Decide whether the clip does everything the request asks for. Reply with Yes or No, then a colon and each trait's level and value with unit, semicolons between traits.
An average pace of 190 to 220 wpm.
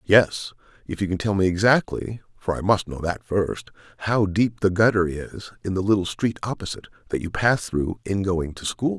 Yes: average, 195 wpm